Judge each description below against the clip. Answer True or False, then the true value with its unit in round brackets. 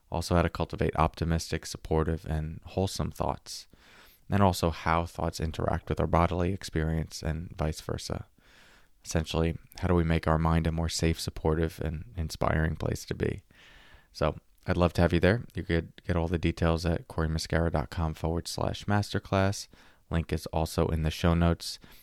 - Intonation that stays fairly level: True (1.6 semitones)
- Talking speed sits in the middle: True (170 wpm)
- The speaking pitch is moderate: False (85 Hz)